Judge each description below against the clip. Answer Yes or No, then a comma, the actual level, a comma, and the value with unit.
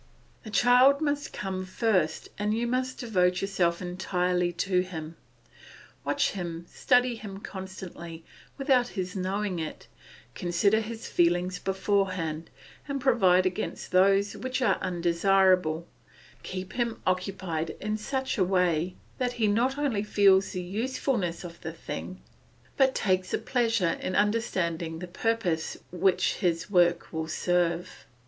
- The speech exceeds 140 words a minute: No, slow, 135 wpm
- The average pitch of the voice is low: No, high, 190 Hz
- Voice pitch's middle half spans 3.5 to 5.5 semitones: Yes, average, 3.9 semitones